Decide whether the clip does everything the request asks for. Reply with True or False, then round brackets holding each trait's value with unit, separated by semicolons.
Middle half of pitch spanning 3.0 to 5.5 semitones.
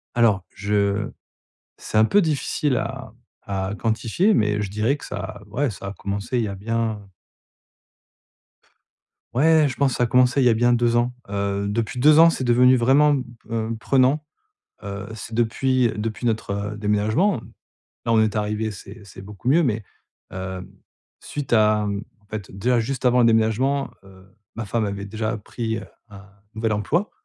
True (3.6 semitones)